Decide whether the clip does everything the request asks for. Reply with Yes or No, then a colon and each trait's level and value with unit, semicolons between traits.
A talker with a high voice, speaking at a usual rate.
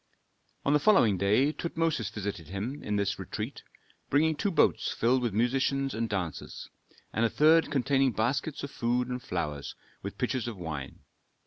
No: low, 120 Hz; average, 160 wpm